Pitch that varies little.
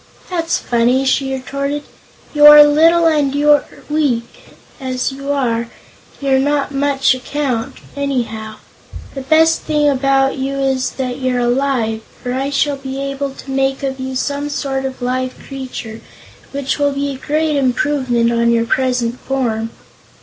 Yes: narrow, 2.1 semitones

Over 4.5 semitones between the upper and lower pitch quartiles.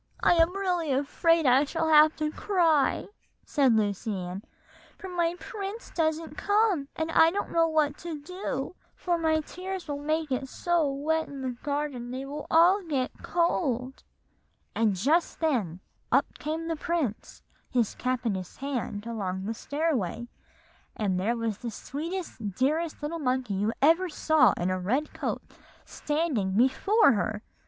Yes: wide, 5.6 semitones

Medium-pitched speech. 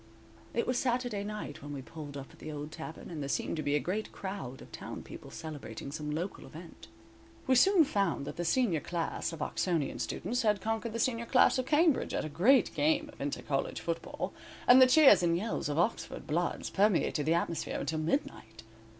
Yes: medium, 175 Hz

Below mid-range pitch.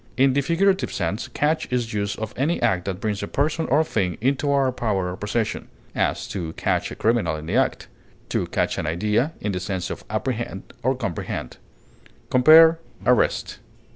Yes: low, 115 Hz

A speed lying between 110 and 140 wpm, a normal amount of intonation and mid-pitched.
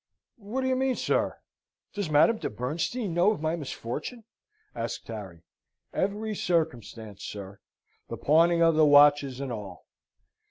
No: slow, 135 wpm; wide, 8.8 semitones; medium, 155 Hz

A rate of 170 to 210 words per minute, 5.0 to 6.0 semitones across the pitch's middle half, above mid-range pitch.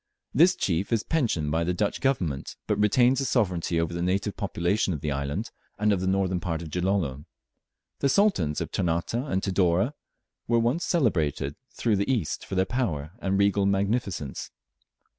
No: average, 175 wpm; wide, 5.4 semitones; very low, 95 Hz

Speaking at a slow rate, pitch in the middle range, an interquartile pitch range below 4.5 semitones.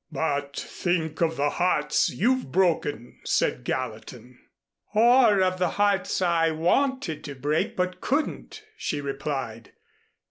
No: slow, 120 wpm; medium, 165 Hz; average, 5.2 semitones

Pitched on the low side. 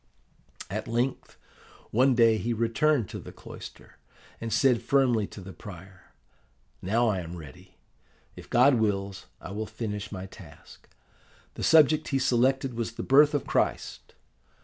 Yes: low, 115 Hz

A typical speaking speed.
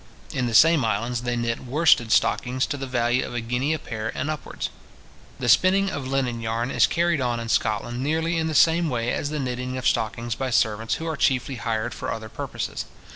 No: fast, 215 wpm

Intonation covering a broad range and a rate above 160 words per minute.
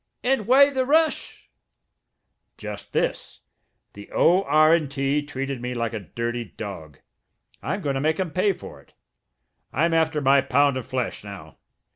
No: wide, 6.1 semitones; average, 150 wpm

